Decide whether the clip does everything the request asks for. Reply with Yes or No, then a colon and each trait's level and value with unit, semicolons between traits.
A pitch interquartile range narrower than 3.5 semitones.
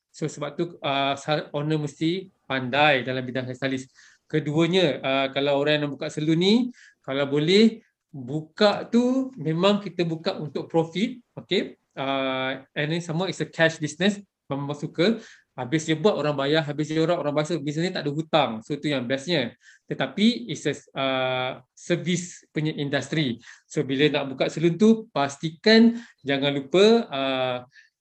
No: average, 4.0 semitones